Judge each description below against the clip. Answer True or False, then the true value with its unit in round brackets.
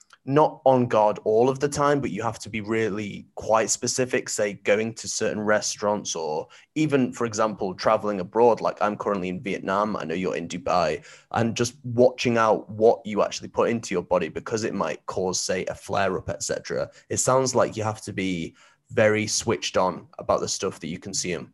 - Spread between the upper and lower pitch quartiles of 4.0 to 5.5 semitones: False (3.1 semitones)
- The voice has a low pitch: True (115 Hz)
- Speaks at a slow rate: False (200 wpm)